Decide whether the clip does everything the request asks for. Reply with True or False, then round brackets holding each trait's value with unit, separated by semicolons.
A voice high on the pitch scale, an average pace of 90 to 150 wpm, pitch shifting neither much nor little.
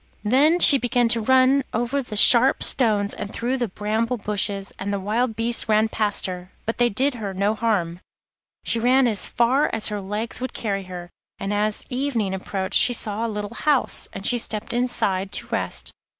False (220 Hz; 195 wpm; 3.3 semitones)